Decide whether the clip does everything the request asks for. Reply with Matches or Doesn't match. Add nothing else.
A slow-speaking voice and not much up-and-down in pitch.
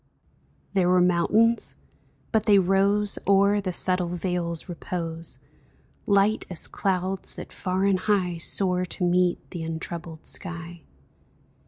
Matches